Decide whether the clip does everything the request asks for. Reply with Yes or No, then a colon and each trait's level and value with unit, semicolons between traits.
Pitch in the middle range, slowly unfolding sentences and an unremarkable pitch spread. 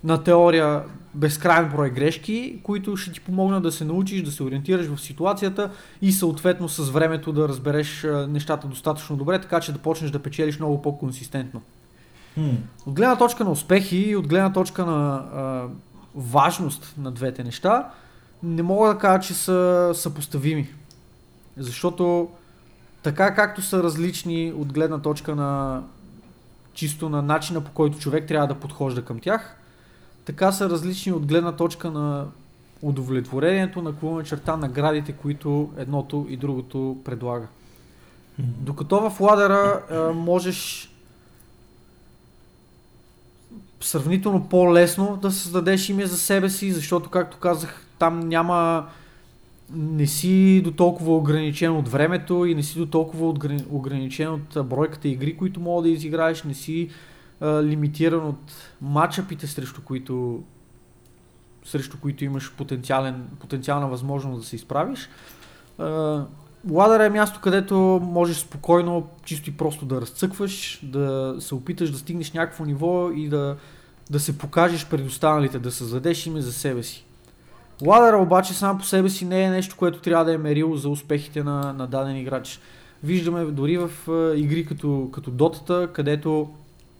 No: medium, 155 Hz; average, 140 wpm; average, 3.7 semitones